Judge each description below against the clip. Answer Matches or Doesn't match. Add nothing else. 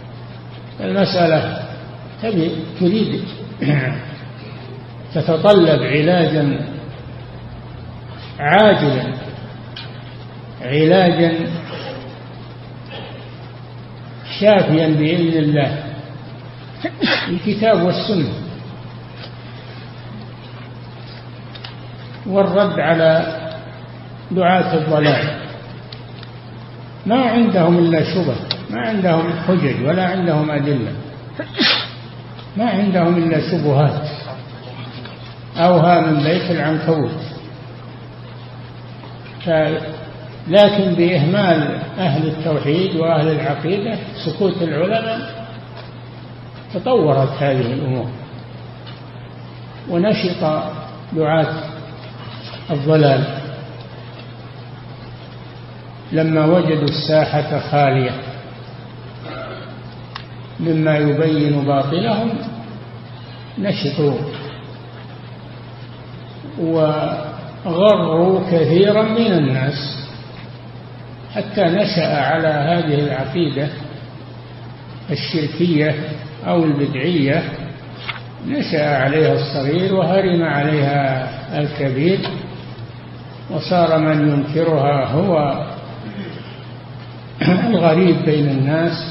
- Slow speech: Matches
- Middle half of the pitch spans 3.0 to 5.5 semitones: Matches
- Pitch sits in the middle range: Matches